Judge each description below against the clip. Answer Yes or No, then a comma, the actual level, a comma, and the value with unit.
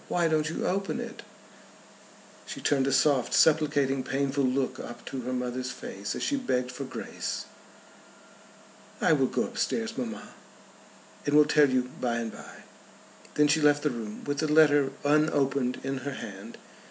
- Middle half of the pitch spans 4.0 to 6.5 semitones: No, average, 2.9 semitones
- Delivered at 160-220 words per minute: Yes, average, 165 wpm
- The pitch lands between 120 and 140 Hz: Yes, low, 135 Hz